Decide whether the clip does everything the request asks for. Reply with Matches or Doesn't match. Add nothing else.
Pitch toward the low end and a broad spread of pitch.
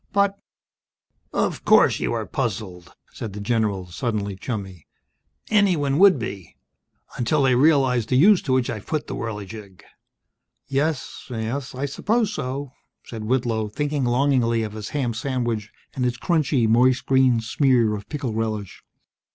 Doesn't match